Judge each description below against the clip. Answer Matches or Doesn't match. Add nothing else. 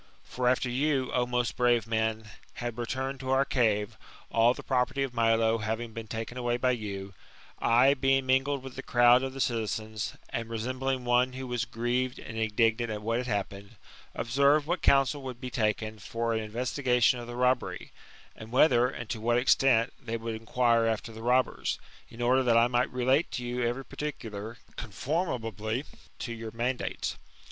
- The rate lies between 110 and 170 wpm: Doesn't match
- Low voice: Matches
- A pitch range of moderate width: Doesn't match